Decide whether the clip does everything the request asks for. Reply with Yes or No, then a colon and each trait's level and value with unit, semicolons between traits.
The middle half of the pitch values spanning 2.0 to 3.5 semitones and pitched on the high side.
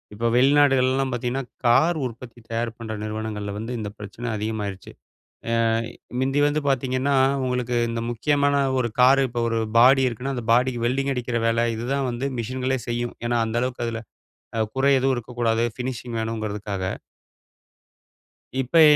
No: narrow, 2.4 semitones; low, 120 Hz